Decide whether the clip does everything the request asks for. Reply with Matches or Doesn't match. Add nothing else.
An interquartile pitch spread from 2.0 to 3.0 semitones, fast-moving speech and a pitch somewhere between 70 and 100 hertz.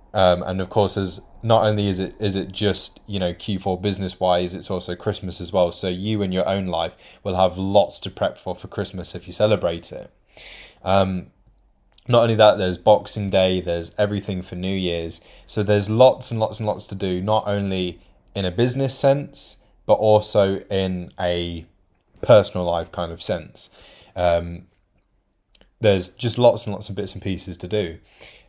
Doesn't match